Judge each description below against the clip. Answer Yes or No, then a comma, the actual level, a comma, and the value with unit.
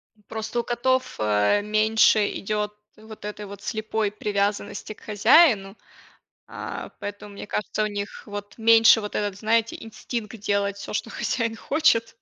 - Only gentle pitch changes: Yes, narrow, 1.7 semitones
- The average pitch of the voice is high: Yes, high, 210 Hz